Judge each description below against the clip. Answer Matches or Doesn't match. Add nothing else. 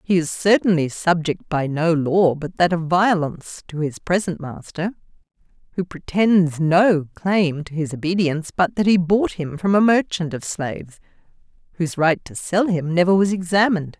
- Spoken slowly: Doesn't match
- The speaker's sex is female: Matches